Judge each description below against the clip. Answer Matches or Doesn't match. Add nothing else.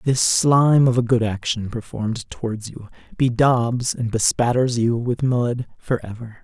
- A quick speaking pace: Doesn't match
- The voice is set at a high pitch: Doesn't match